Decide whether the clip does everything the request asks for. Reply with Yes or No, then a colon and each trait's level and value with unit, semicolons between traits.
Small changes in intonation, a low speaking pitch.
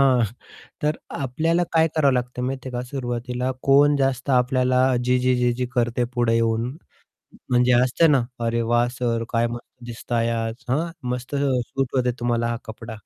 Yes: narrow, 2.0 semitones; low, 125 Hz